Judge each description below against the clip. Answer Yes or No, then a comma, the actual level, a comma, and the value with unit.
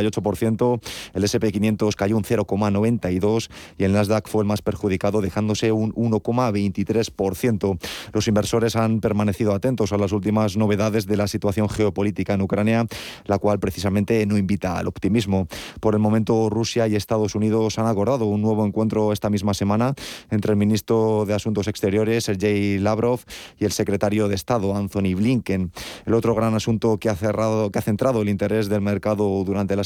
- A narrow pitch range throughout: Yes, narrow, 1.5 semitones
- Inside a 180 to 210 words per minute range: No, average, 170 wpm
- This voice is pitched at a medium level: No, low, 105 Hz